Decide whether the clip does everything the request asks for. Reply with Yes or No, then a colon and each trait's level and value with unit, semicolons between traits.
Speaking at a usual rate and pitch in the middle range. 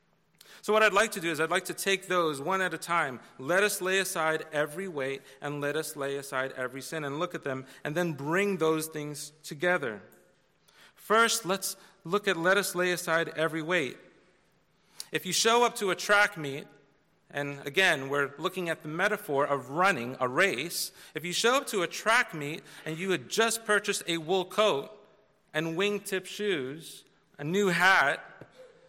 Yes: average, 185 wpm; medium, 175 Hz